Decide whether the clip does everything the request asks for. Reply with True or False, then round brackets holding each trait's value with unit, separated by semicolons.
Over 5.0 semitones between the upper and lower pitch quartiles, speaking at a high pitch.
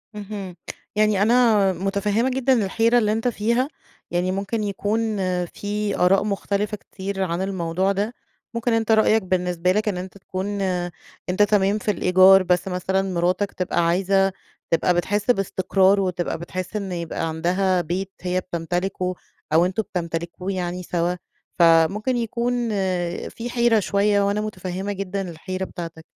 False (2.6 semitones; 195 Hz)